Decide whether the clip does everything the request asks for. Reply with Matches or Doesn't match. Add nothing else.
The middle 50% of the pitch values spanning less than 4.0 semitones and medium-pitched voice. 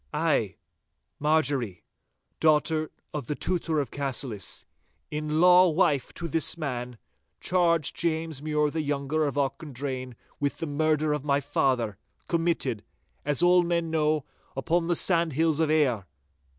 Matches